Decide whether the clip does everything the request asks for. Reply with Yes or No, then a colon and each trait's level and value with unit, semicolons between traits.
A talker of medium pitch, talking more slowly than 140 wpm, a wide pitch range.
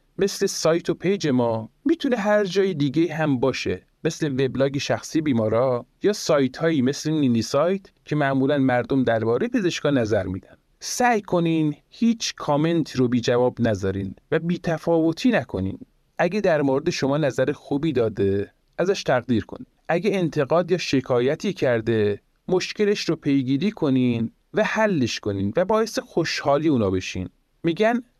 No: medium, 150 Hz; average, 145 wpm; wide, 6.6 semitones